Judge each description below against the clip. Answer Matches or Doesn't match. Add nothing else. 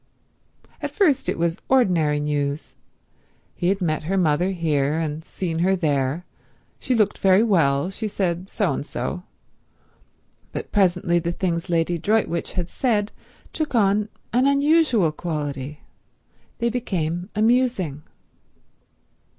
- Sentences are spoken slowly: Matches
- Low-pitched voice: Doesn't match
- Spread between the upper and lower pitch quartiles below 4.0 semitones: Doesn't match